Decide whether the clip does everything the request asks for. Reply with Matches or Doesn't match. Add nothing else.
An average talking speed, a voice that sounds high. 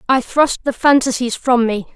Matches